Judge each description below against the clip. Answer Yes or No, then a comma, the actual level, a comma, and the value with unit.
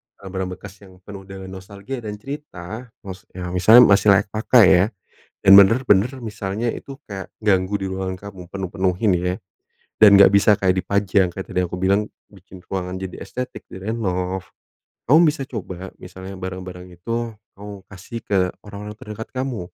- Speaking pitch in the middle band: No, very low, 95 Hz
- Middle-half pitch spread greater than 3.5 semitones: No, narrow, 2.5 semitones